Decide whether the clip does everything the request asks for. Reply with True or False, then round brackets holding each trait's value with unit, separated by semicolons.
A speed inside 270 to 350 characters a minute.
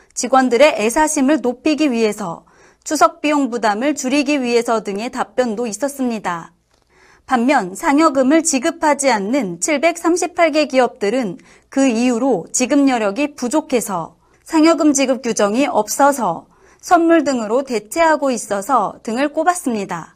True (290 characters per minute)